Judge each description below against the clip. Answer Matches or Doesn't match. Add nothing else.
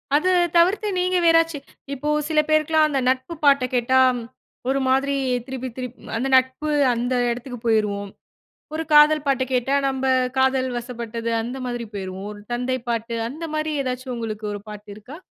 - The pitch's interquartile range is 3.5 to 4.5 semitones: Matches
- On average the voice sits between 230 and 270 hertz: Matches